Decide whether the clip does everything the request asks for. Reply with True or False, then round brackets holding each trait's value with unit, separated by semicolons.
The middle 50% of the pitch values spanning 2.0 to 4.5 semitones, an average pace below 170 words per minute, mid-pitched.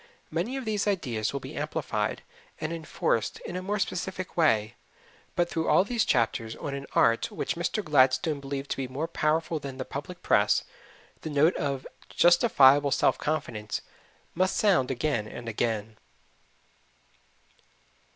False (5.2 semitones; 150 wpm; 145 Hz)